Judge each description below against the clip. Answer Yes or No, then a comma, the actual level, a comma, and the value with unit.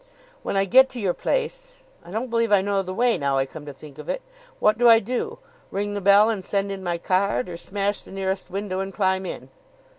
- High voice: Yes, high, 200 Hz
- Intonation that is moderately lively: Yes, average, 3.3 semitones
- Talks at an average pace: No, fast, 240 wpm